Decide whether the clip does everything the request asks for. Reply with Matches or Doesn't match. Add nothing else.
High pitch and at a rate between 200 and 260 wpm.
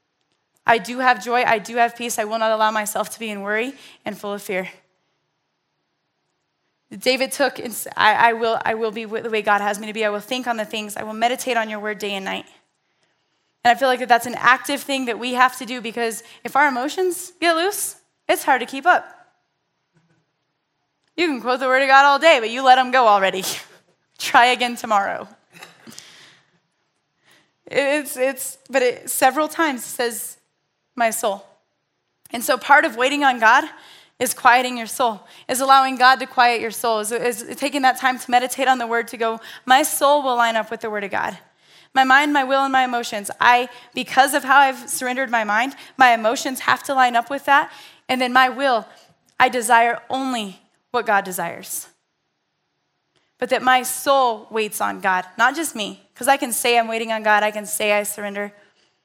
Matches